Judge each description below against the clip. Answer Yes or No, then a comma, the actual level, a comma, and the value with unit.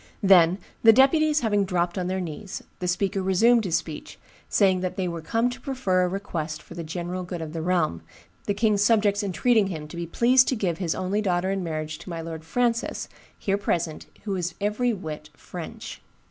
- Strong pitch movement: No, average, 3.6 semitones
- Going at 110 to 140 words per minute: No, average, 200 wpm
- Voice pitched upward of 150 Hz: Yes, medium, 185 Hz